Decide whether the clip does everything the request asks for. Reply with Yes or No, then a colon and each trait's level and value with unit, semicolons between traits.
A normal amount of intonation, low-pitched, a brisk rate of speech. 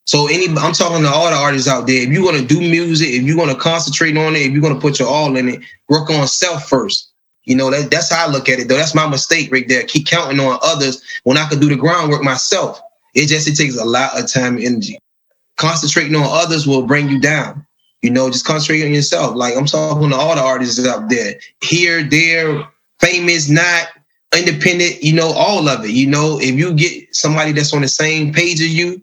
No: average, 3.3 semitones; medium, 150 Hz; fast, 240 wpm